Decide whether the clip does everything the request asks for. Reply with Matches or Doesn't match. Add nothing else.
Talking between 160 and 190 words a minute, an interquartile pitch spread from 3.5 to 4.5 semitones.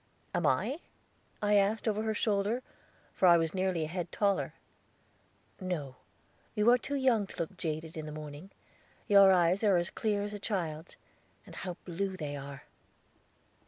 Matches